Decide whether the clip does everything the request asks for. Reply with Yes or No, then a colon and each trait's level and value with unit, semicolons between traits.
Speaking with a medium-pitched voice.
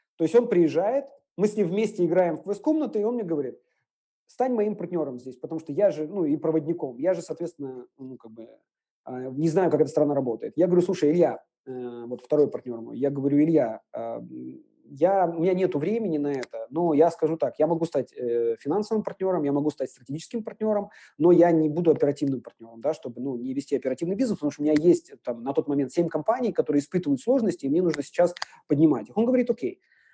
Yes: medium, 160 Hz